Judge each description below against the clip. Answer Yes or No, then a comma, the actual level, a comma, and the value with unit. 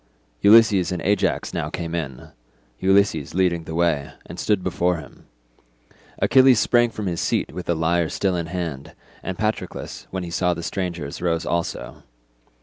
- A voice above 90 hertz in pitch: No, very low, 85 Hz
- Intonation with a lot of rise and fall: No, narrow, 2.6 semitones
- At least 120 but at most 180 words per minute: Yes, average, 155 wpm